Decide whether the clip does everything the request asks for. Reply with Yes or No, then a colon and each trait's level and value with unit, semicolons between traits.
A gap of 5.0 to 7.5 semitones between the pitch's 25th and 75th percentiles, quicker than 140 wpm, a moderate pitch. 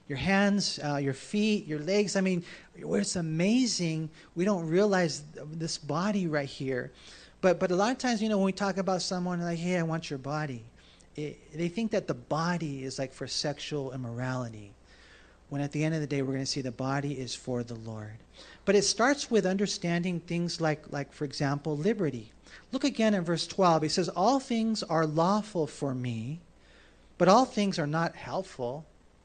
Yes: average, 5.3 semitones; average, 195 wpm; medium, 165 Hz